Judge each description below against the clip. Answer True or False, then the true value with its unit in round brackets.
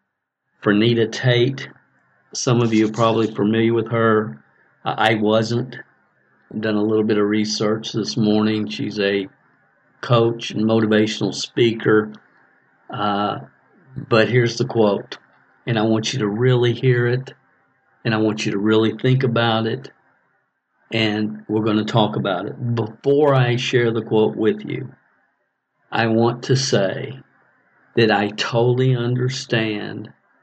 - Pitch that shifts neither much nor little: False (2.1 semitones)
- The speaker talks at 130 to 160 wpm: True (140 wpm)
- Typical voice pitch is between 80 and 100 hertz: False (110 Hz)